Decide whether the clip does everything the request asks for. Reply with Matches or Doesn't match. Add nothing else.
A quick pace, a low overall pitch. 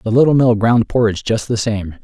Matches